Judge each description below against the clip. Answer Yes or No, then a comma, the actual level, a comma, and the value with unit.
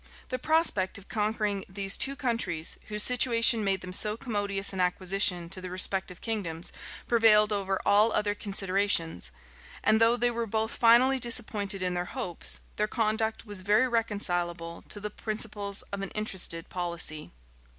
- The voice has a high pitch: Yes, high, 205 Hz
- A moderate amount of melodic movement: Yes, average, 3.2 semitones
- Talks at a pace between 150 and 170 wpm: Yes, average, 155 wpm